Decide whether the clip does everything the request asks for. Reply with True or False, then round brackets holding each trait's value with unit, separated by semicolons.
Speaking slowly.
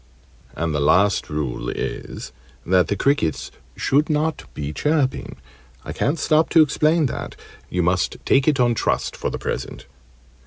False (155 wpm)